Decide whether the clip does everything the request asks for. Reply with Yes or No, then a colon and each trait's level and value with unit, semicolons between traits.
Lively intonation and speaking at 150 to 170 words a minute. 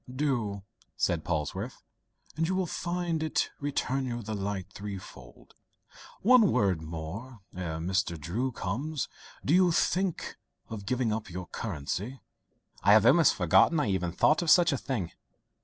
Yes: wide, 8.4 semitones; average, 155 wpm